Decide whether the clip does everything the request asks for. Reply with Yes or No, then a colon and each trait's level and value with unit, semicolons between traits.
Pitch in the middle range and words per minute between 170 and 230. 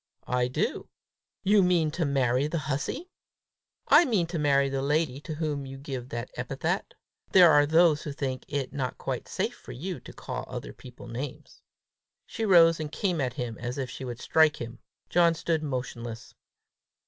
Yes: medium, 145 Hz; average, 180 wpm